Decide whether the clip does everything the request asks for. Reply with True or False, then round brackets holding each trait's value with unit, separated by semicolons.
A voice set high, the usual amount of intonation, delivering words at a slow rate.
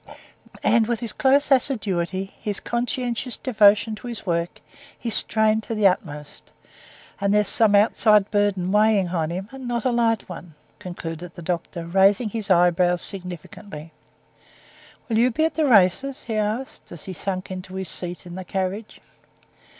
False (205 Hz; 4.1 semitones; 160 wpm)